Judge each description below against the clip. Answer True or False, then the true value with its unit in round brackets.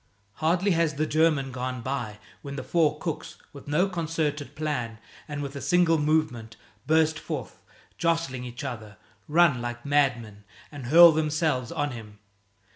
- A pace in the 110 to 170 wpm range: True (150 wpm)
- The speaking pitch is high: False (145 Hz)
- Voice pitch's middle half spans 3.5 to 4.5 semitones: True (4.0 semitones)